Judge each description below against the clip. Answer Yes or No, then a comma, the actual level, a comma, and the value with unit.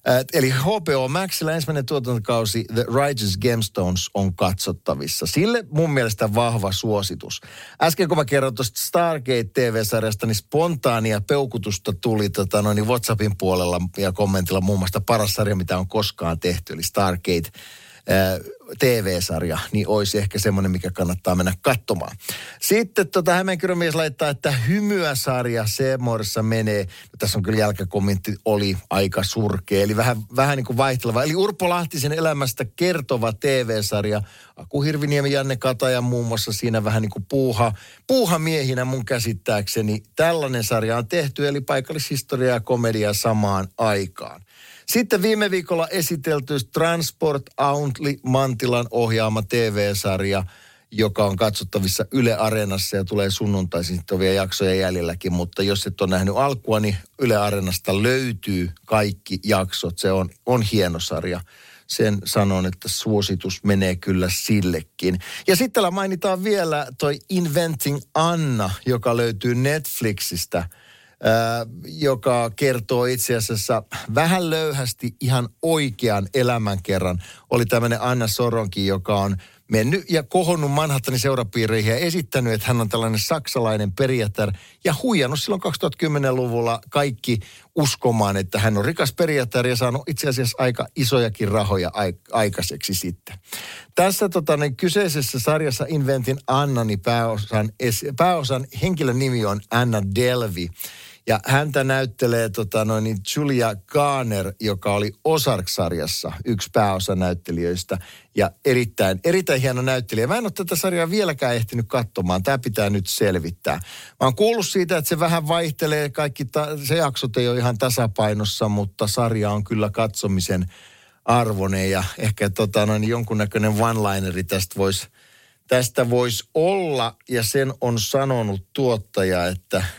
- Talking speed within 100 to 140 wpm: Yes, average, 135 wpm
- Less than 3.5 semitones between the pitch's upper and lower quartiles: No, wide, 5.4 semitones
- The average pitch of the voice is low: Yes, low, 115 Hz